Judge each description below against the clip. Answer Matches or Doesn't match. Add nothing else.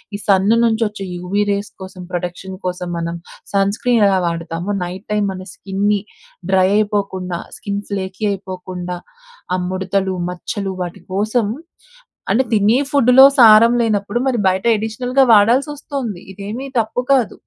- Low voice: Doesn't match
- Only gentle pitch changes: Doesn't match